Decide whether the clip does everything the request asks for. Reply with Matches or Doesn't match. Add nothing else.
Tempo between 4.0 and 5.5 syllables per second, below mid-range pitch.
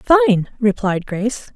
Doesn't match